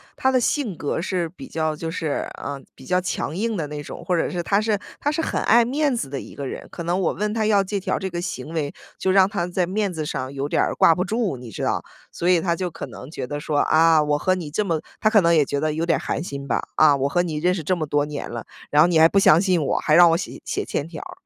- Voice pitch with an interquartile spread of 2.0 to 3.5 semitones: No, average, 4.2 semitones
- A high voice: No, medium, 170 Hz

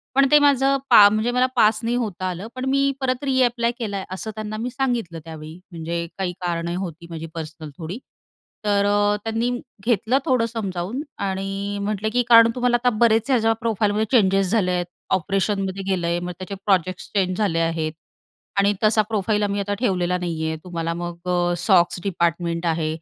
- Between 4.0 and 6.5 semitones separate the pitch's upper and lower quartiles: Yes, average, 4.5 semitones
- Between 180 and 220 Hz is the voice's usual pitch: Yes, high, 200 Hz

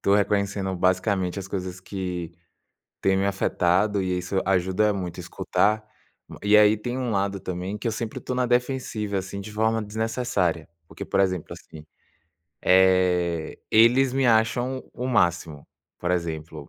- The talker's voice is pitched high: No, low, 100 Hz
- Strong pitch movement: No, average, 3.3 semitones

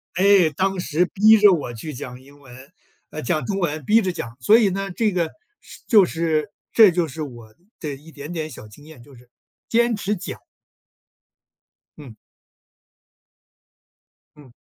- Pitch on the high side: No, medium, 160 Hz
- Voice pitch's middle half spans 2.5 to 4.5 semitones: No, wide, 5.6 semitones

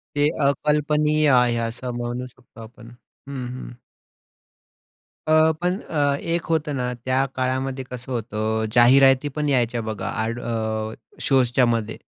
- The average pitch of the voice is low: Yes, low, 125 Hz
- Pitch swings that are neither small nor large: Yes, average, 3.4 semitones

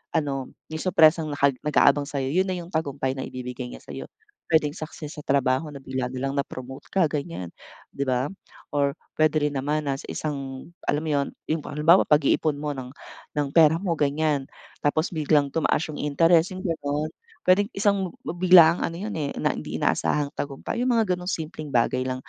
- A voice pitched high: No, medium, 150 Hz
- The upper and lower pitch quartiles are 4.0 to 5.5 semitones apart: No, average, 2.9 semitones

